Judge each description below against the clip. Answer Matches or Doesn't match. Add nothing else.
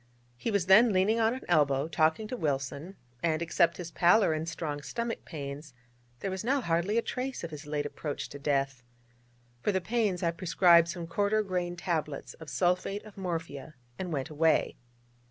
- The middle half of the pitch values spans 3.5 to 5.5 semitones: Matches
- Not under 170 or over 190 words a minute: Matches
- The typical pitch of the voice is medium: Matches